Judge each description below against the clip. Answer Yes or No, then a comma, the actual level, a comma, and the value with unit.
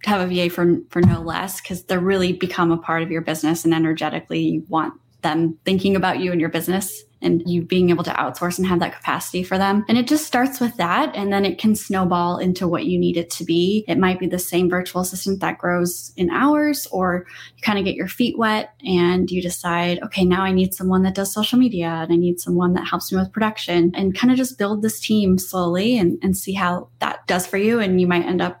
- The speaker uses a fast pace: Yes, fast, 250 wpm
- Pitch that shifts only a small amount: Yes, narrow, 2.1 semitones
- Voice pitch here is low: No, medium, 180 Hz